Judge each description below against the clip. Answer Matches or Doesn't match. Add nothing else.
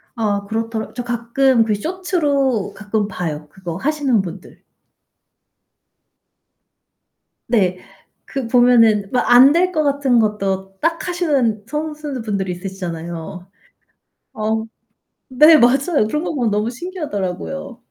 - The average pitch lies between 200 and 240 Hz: Matches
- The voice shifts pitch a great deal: Matches